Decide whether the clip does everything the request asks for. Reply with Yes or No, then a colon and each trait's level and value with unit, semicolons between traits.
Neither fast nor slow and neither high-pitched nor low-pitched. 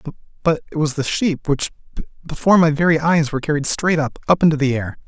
Yes: average, 190 wpm; medium, 150 Hz